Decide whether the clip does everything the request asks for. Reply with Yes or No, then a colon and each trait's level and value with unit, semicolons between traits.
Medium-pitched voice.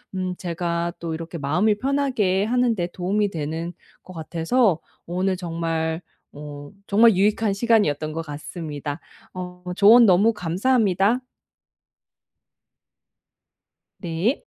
Yes: medium, 180 Hz